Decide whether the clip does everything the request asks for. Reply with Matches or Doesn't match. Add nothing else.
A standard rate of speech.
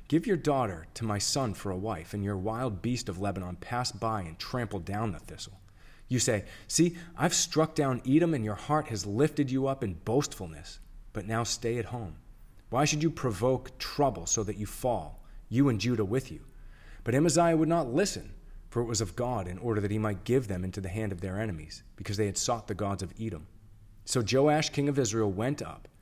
Doesn't match